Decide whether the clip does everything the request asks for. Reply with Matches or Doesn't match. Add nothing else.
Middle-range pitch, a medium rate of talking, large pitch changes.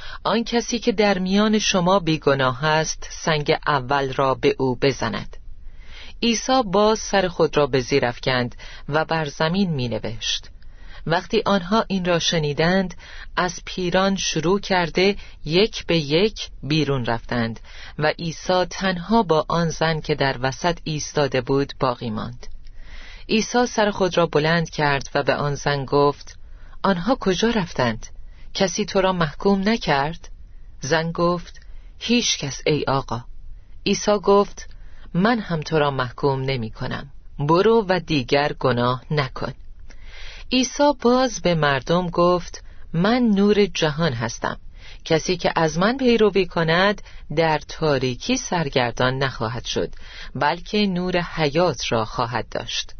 Matches